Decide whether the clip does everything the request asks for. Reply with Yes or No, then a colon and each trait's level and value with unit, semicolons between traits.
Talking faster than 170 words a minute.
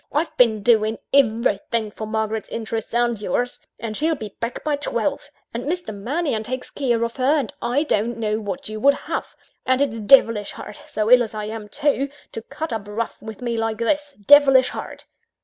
Yes: average, 195 wpm